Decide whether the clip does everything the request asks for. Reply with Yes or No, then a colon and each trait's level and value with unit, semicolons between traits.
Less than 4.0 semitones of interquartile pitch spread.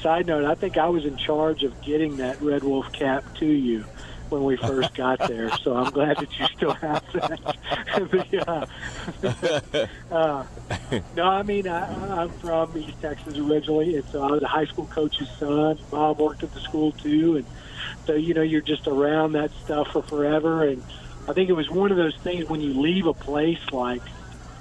Yes: average, 2.7 semitones